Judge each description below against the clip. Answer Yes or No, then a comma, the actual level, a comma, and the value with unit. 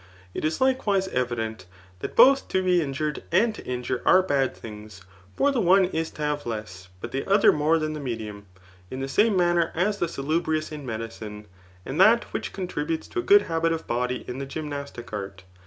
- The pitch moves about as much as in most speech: No, wide, 7.1 semitones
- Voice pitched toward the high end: No, medium, 150 Hz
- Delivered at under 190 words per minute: No, fast, 205 wpm